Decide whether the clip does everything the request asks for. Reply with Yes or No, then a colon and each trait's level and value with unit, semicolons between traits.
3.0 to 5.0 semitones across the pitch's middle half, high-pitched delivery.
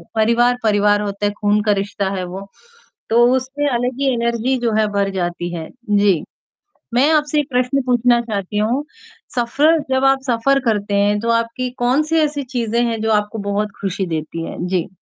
Yes: average, 3.7 semitones; high, 230 Hz